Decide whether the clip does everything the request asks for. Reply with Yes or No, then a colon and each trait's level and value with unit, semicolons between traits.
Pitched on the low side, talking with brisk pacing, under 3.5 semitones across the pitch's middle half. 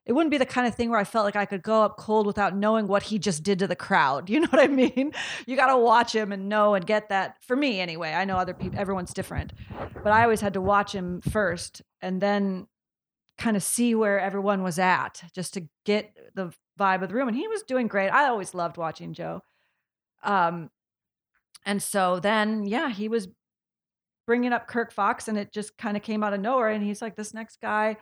No: high, 210 Hz; fast, 235 wpm; average, 3.1 semitones